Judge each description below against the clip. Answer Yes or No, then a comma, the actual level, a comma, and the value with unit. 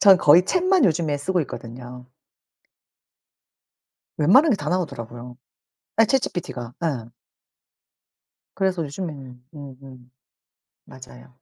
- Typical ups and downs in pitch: No, wide, 6.8 semitones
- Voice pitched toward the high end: No, medium, 145 Hz